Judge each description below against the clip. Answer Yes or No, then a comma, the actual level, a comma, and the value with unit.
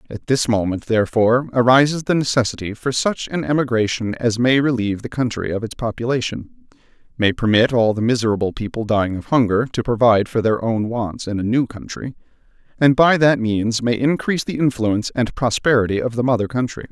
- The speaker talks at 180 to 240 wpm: Yes, average, 185 wpm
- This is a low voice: Yes, low, 120 Hz